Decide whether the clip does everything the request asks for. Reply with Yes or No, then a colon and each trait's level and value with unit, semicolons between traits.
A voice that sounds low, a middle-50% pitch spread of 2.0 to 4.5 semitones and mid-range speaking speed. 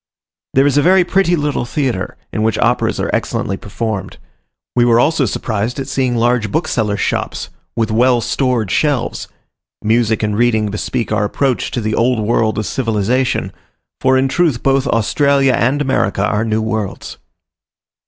Yes: low, 120 Hz; average, 3.7 semitones; average, 160 wpm